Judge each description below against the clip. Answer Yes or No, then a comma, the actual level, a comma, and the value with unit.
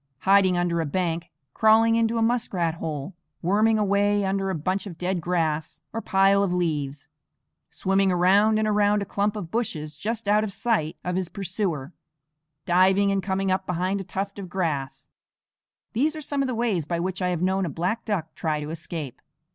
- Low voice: No, high, 190 Hz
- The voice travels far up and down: No, average, 3.4 semitones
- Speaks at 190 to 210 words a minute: Yes, average, 195 wpm